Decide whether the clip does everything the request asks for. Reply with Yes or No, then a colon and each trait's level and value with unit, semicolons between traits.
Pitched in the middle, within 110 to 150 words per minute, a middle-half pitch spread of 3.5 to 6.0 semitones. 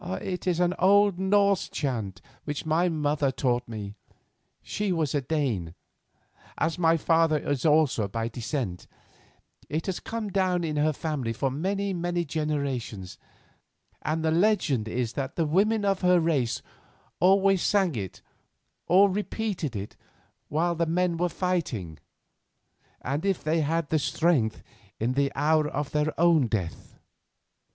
Yes: medium, 160 Hz; average, 145 wpm; average, 5.2 semitones